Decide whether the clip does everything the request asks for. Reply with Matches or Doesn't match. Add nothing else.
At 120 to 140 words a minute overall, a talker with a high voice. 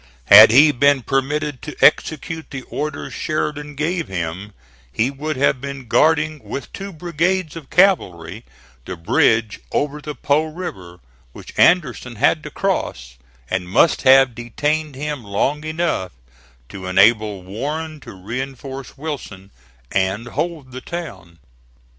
Doesn't match